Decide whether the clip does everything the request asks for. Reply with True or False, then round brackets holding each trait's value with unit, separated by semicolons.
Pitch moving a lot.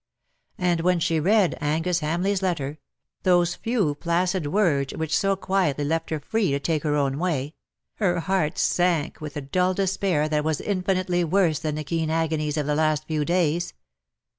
False (3.3 semitones)